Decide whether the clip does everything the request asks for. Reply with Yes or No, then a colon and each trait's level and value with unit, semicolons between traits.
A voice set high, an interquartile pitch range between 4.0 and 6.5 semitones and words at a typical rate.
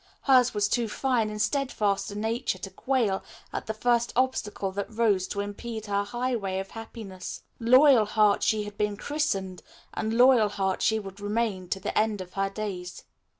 No: high, 210 Hz; average, 3.1 semitones; average, 170 wpm